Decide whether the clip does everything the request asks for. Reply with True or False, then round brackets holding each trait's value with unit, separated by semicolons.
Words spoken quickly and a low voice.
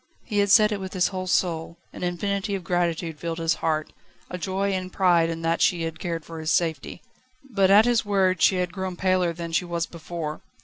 False (220 wpm; 180 Hz)